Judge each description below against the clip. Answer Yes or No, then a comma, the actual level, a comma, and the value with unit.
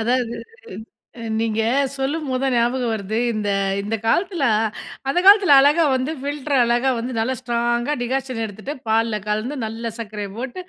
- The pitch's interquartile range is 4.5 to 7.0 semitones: No, average, 3.3 semitones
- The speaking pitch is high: Yes, high, 240 Hz